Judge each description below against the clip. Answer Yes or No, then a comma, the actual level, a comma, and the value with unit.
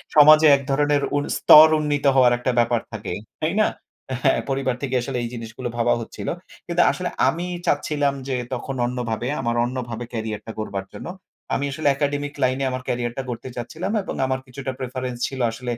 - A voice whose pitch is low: Yes, low, 130 Hz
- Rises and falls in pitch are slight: No, average, 3.1 semitones